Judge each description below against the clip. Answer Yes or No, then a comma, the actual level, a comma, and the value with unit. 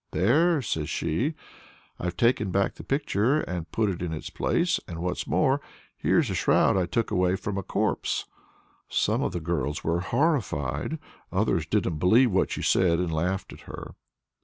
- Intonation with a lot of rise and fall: Yes, wide, 5.7 semitones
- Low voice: Yes, very low, 95 Hz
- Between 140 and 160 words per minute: No, average, 175 wpm